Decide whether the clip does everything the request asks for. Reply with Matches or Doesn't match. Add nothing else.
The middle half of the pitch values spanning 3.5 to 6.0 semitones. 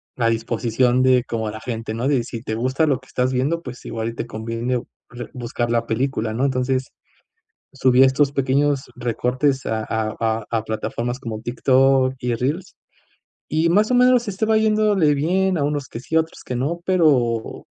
Matches